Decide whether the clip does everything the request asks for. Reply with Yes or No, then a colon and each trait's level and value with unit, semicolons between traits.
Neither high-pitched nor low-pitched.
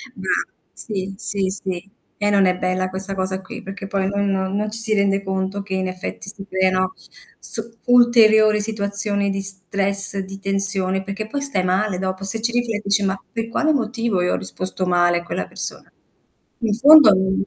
No: high, 195 Hz